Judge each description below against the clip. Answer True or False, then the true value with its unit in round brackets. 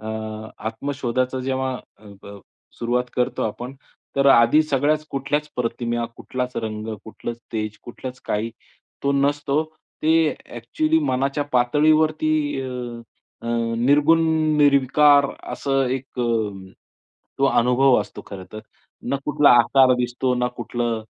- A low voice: True (130 Hz)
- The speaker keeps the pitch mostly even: False (3.2 semitones)